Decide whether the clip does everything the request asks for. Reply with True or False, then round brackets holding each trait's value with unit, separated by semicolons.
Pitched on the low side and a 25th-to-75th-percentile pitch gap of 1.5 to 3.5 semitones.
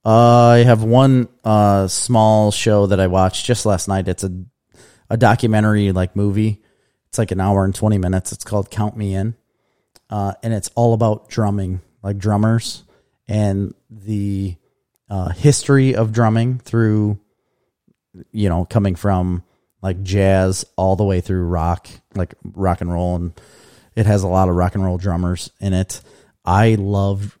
True (100 Hz; 2.8 semitones)